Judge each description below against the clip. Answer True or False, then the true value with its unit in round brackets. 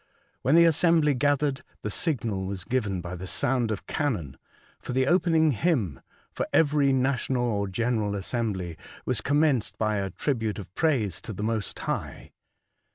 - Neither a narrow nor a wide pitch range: False (6.2 semitones)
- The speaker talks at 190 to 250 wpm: False (160 wpm)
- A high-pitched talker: False (120 Hz)